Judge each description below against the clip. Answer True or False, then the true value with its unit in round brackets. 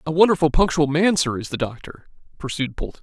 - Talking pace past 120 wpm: True (200 wpm)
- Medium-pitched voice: True (155 Hz)